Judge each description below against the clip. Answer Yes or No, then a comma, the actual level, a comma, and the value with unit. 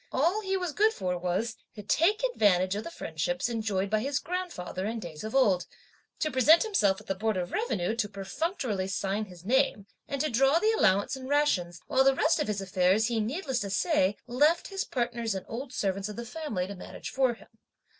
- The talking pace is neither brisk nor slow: No, fast, 210 wpm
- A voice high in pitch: Yes, high, 225 Hz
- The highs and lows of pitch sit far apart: Yes, wide, 7.1 semitones